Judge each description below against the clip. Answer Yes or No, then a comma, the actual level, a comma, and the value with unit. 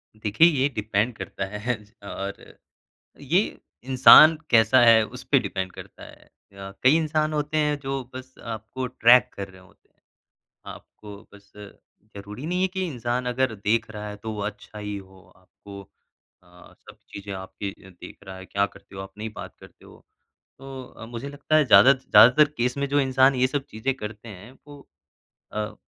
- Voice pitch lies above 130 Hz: No, low, 115 Hz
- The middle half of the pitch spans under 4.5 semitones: No, average, 4.9 semitones